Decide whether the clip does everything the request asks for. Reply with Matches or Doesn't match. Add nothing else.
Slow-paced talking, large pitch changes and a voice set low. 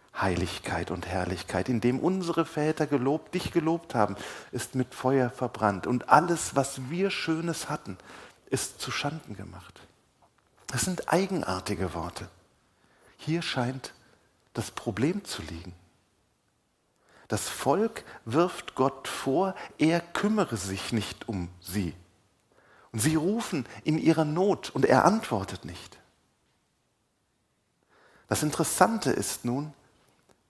Matches